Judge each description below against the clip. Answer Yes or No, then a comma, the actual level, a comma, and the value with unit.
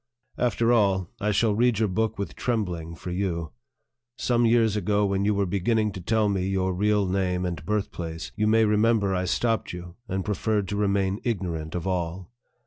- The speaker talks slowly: No, average, 185 wpm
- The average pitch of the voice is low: Yes, low, 100 Hz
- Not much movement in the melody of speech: No, average, 3.0 semitones